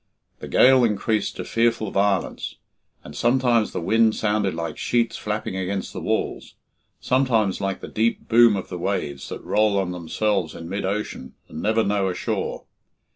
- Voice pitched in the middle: No, low, 105 Hz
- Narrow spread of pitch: No, average, 3.2 semitones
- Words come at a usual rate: Yes, average, 170 wpm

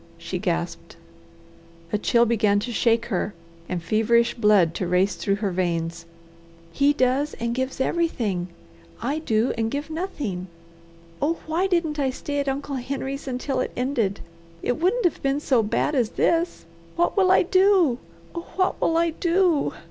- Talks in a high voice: Yes, very high, 260 Hz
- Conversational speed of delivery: Yes, average, 165 wpm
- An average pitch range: No, wide, 6.8 semitones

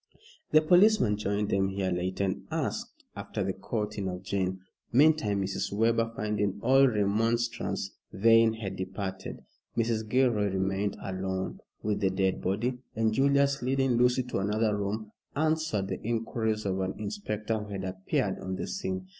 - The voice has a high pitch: No, low, 105 Hz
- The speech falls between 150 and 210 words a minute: Yes, average, 155 wpm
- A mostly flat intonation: No, average, 3.5 semitones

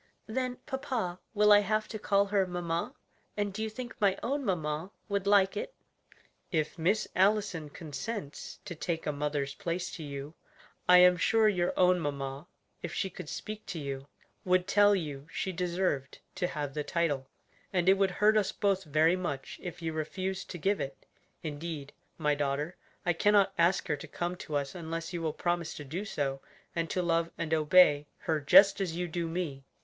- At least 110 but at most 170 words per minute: No, average, 190 wpm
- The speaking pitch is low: No, medium, 175 Hz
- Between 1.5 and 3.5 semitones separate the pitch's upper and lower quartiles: No, average, 4.4 semitones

